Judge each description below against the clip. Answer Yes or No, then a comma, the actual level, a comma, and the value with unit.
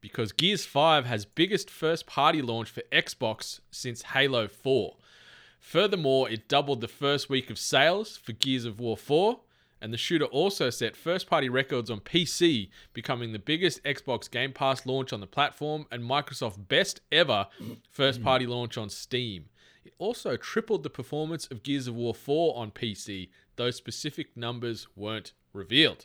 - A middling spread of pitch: Yes, average, 4.1 semitones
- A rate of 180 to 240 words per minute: No, average, 165 wpm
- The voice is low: Yes, low, 130 Hz